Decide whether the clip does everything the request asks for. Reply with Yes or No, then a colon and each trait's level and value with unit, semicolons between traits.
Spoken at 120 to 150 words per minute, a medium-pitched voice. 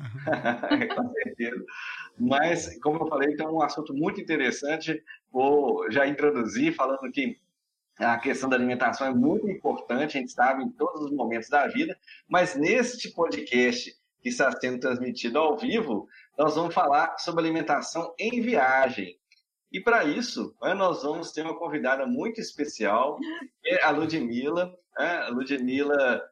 Yes: average, 145 wpm; medium, 155 Hz